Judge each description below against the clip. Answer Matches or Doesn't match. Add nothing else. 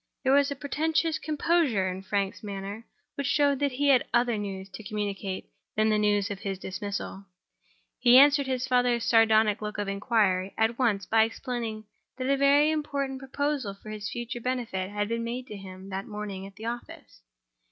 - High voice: Matches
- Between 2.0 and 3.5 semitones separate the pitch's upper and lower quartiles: Doesn't match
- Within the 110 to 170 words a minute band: Doesn't match